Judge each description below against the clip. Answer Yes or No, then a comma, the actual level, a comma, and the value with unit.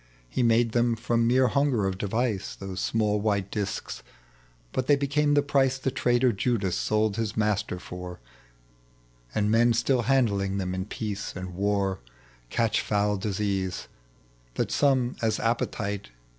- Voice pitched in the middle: No, low, 110 Hz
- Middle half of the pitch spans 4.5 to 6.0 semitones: No, average, 3.5 semitones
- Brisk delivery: No, average, 145 wpm